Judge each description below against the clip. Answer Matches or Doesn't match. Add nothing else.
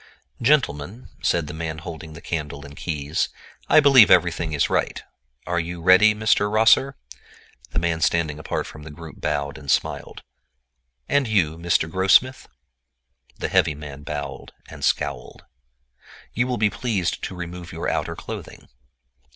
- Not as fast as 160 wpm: Matches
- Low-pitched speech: Matches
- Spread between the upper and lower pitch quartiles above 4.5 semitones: Matches